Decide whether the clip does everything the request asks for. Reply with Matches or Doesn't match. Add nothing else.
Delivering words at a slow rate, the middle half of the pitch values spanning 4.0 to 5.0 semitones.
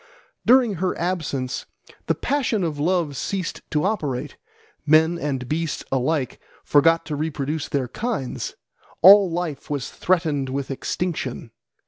Matches